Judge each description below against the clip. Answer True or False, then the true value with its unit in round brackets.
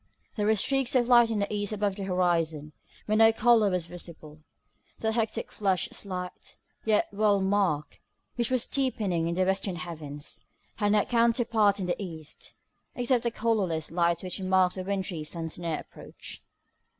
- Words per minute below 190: True (165 wpm)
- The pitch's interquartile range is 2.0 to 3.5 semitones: False (4.3 semitones)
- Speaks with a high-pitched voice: True (195 Hz)